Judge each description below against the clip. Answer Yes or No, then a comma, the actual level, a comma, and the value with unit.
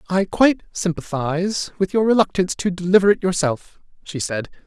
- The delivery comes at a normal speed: Yes, average, 155 wpm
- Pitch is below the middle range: No, medium, 180 Hz